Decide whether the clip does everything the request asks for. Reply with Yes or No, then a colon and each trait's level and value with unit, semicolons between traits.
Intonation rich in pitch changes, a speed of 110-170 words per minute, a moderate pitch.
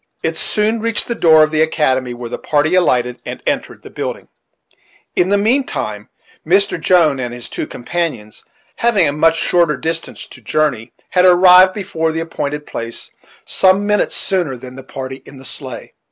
No: wide, 5.9 semitones; average, 180 wpm; medium, 160 Hz